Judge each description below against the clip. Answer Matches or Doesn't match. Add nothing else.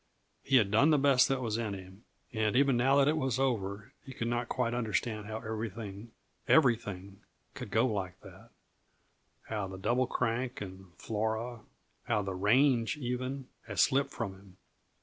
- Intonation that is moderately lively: Matches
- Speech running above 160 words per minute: Matches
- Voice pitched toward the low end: Matches